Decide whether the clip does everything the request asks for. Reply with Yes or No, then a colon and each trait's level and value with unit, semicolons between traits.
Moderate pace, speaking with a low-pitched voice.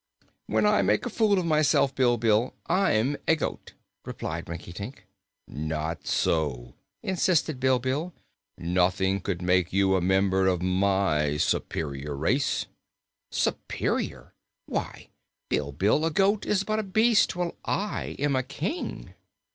No: slow, 125 wpm; low, 105 Hz